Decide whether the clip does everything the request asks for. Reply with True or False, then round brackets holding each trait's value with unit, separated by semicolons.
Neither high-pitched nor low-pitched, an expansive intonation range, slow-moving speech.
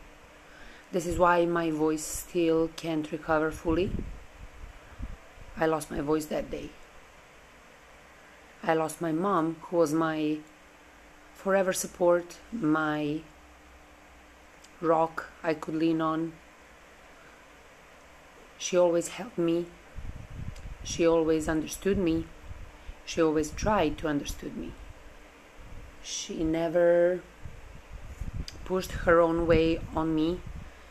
True (160 Hz; 7.9 semitones; 100 wpm)